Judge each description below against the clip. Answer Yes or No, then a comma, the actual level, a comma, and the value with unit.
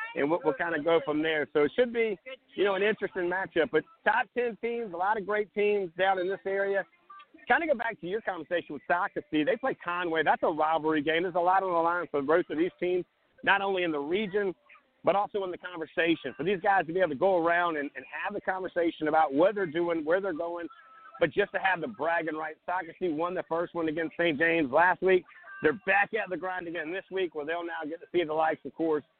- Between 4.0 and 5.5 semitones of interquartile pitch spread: No, average, 3.4 semitones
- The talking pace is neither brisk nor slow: No, fast, 255 wpm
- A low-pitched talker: No, medium, 180 Hz